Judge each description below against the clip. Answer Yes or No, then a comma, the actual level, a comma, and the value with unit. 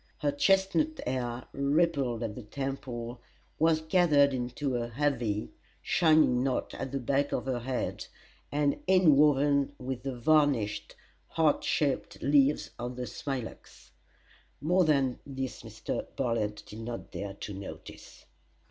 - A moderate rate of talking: No, slow, 130 wpm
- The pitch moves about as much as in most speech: Yes, average, 3.4 semitones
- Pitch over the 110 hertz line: Yes, low, 135 Hz